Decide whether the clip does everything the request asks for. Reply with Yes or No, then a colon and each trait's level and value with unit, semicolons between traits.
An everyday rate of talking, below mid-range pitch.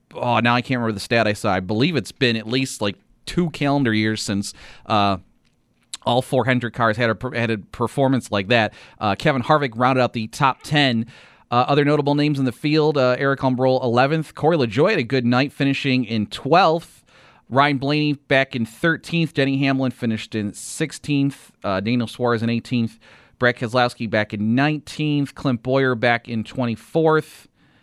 Yes: average, 180 wpm; low, 125 Hz